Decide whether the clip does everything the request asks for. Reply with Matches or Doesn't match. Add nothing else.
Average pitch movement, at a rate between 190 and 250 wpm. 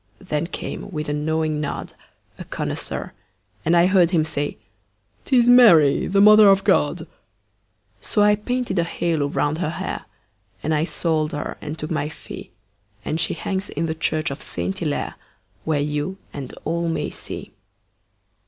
Doesn't match